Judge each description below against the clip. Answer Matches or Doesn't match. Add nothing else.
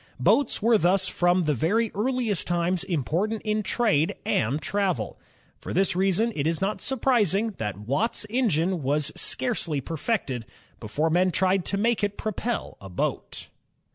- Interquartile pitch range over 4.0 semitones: Matches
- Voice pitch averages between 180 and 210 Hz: Matches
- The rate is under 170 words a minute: Matches